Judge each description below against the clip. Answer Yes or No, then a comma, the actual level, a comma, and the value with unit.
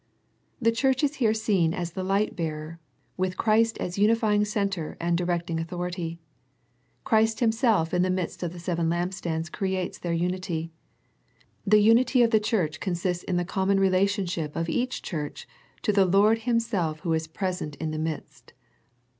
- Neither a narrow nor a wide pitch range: Yes, average, 4.1 semitones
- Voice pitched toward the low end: No, medium, 185 Hz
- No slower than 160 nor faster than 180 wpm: Yes, average, 170 wpm